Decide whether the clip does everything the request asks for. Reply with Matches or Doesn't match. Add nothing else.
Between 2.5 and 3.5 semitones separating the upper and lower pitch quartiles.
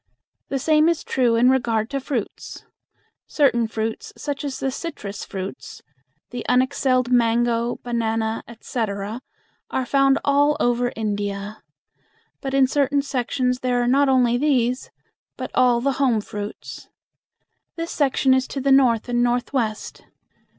Matches